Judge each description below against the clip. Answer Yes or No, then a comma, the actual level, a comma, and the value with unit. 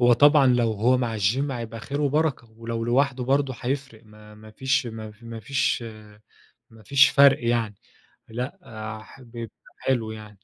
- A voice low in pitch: Yes, low, 120 Hz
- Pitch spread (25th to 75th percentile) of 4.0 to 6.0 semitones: No, average, 3.3 semitones